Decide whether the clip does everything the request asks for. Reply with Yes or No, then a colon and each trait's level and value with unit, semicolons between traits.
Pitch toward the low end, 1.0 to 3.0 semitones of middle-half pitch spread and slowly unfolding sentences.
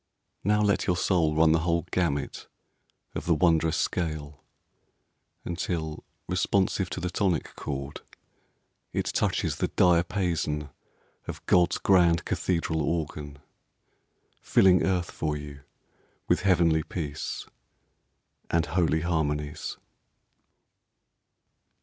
Yes: very low, 85 Hz; average, 2.7 semitones; slow, 100 wpm